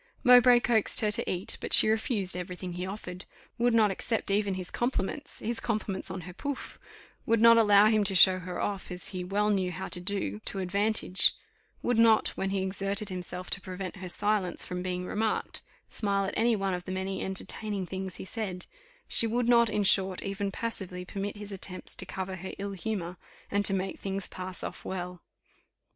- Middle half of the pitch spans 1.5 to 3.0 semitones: Yes, narrow, 2.6 semitones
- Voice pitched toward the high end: Yes, high, 195 Hz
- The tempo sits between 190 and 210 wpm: Yes, average, 200 wpm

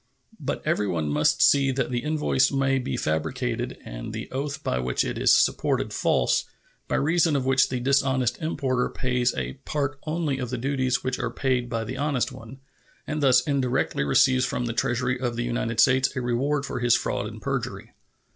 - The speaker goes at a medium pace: Yes, average, 190 wpm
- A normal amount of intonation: No, narrow, 2.2 semitones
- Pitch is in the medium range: No, low, 130 Hz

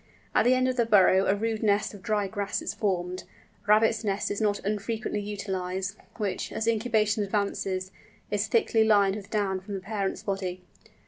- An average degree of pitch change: No, narrow, 2.0 semitones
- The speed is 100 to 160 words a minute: No, average, 175 wpm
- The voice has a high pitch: Yes, high, 205 Hz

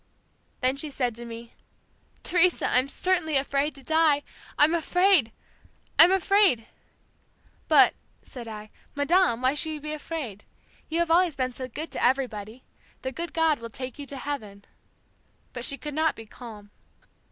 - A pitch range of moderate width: Yes, average, 4.9 semitones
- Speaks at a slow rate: No, average, 160 wpm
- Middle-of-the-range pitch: No, very high, 280 Hz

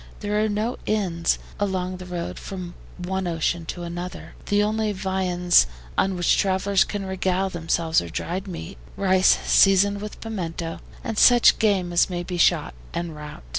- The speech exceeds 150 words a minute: Yes, average, 165 wpm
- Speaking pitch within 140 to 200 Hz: Yes, medium, 185 Hz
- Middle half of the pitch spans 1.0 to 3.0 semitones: Yes, narrow, 2.6 semitones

